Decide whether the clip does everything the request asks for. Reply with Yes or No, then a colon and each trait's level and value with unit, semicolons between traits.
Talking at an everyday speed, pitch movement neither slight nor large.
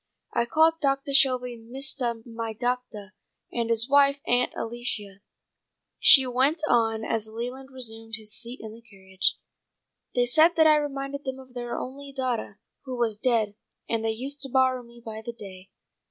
Yes: average, 170 wpm; average, 3.1 semitones